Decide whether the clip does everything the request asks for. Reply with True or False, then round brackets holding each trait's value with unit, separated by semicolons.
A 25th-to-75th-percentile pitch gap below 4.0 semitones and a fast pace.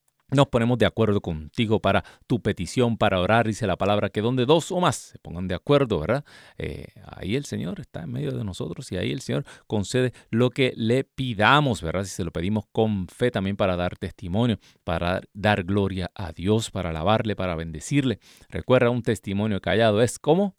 False (4.6 semitones; 195 wpm)